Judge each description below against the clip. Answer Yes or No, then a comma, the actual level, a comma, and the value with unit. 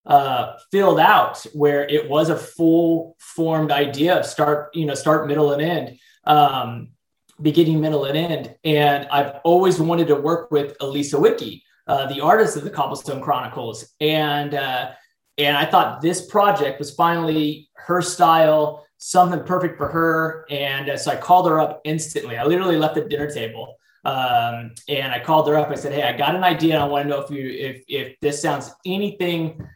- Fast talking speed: No, average, 185 wpm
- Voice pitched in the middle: Yes, medium, 150 Hz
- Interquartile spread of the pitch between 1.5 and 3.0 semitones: Yes, narrow, 2.6 semitones